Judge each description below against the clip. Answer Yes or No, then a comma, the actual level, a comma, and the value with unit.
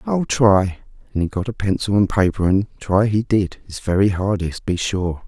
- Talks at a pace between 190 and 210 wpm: Yes, fast, 205 wpm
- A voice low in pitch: Yes, low, 100 Hz